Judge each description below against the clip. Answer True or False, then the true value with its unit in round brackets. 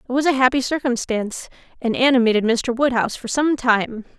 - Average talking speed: True (170 wpm)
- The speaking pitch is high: True (245 Hz)